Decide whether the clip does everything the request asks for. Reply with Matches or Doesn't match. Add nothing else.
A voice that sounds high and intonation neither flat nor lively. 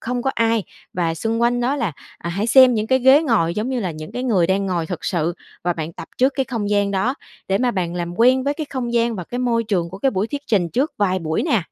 Doesn't match